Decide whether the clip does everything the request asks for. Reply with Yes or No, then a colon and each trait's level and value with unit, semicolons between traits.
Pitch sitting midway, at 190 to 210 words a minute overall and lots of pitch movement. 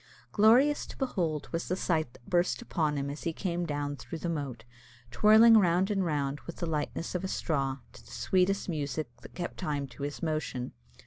No: medium, 165 Hz; average, 200 wpm; average, 4.3 semitones